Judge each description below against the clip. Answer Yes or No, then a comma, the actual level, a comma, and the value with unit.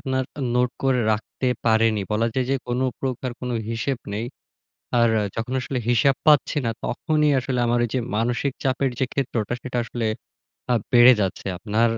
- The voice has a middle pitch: No, low, 125 Hz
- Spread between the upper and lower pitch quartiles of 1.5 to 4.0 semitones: Yes, narrow, 2.4 semitones